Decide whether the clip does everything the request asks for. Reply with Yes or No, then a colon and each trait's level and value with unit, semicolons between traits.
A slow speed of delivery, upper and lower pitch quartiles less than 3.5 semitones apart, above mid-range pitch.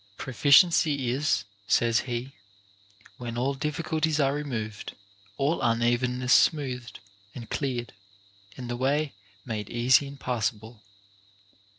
No: slow, 110 wpm; average, 3.1 semitones; low, 125 Hz